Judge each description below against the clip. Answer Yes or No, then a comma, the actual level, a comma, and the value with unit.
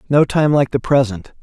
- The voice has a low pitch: Yes, low, 130 Hz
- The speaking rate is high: Yes, fast, 210 wpm